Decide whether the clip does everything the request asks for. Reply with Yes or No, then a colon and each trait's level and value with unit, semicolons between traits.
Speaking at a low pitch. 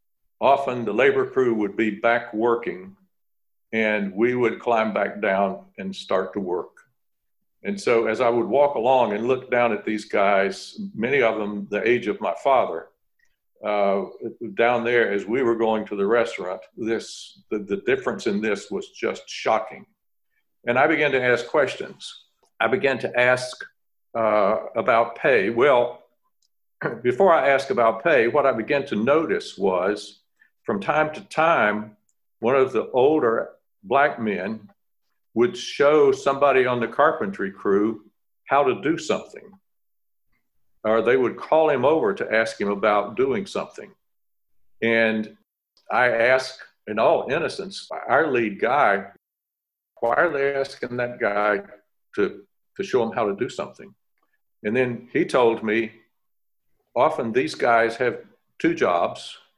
Yes: low, 120 Hz